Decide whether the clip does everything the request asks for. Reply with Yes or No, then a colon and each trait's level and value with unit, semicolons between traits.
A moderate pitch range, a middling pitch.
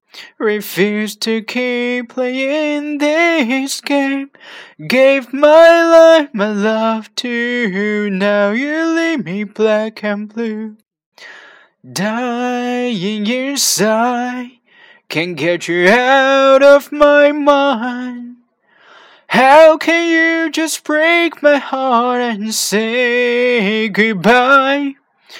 No: average, 5.0 semitones; high, 245 Hz